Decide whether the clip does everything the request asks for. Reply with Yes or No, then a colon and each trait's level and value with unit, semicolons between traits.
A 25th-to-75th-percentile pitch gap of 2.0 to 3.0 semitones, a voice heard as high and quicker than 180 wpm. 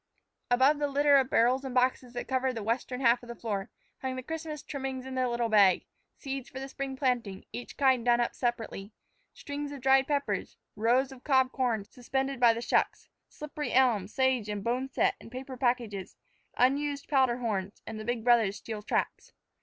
Yes: narrow, 2.4 semitones; very high, 255 Hz; average, 190 wpm